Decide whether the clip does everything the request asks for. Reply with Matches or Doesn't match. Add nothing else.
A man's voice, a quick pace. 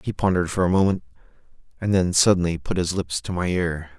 Matches